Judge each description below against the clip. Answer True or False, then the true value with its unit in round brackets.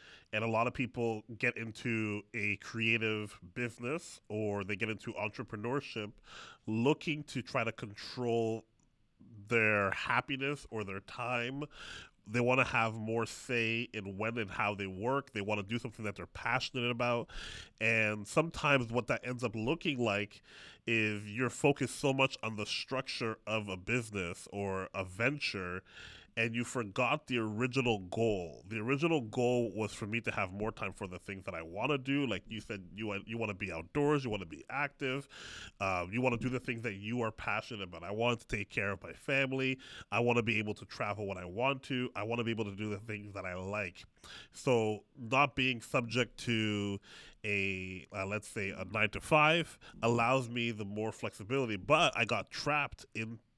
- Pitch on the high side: False (115 Hz)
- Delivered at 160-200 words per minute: True (195 wpm)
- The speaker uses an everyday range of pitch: True (3.2 semitones)